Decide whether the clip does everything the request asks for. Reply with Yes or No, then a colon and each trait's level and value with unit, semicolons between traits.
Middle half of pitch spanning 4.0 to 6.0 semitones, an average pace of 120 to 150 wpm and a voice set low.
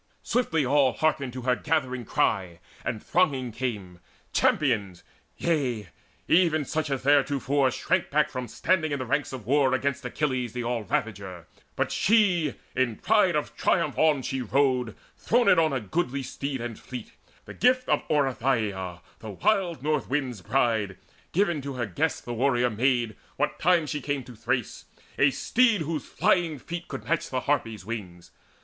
No: average, 4.5 semitones; average, 160 wpm; low, 130 Hz